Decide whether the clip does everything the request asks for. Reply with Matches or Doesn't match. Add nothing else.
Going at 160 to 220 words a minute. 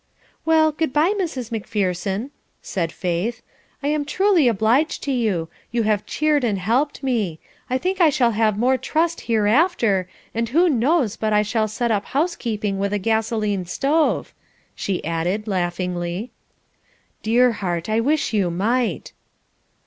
Doesn't match